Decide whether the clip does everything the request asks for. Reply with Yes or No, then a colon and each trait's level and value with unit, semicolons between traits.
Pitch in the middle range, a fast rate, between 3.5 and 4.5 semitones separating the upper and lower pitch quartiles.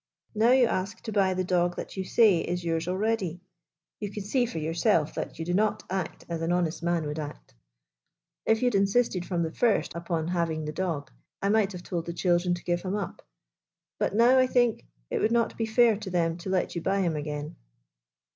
Yes: medium, 180 Hz; fast, 220 wpm; average, 3.9 semitones